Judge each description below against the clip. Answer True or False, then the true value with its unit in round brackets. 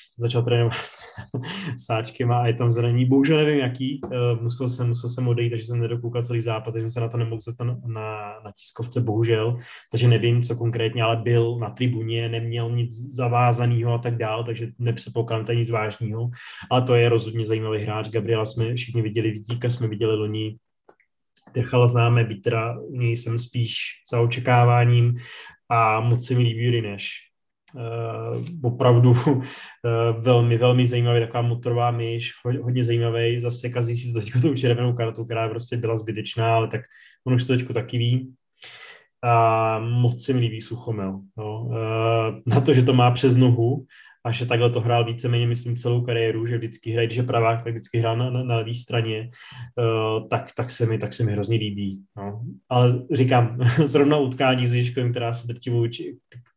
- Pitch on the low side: True (120 Hz)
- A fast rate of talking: True (175 wpm)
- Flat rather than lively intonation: True (1.2 semitones)